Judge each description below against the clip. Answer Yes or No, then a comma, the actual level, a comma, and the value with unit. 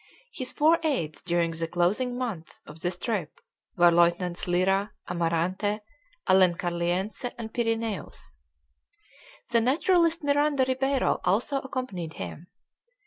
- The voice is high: Yes, high, 195 Hz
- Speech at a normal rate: No, slow, 110 wpm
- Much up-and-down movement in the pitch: Yes, wide, 6.8 semitones